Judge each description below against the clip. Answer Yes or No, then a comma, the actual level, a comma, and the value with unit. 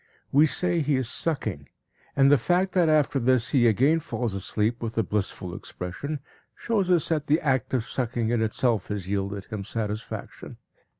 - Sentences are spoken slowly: No, average, 175 wpm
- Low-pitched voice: Yes, low, 125 Hz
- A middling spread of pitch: No, wide, 6.0 semitones